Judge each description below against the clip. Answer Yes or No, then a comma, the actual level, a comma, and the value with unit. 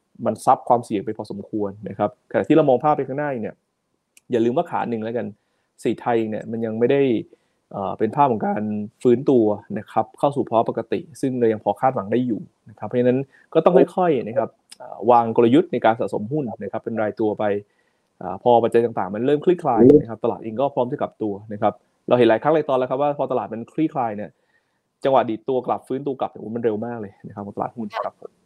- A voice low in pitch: Yes, low, 120 Hz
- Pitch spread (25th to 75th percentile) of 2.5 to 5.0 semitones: Yes, average, 3.9 semitones